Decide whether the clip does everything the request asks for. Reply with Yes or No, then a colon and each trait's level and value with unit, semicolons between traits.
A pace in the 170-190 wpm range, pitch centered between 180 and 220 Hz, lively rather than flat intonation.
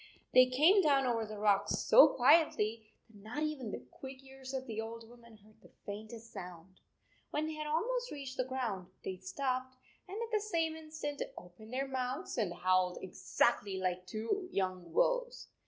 No: average, 175 wpm; very high, 250 Hz; wide, 6.4 semitones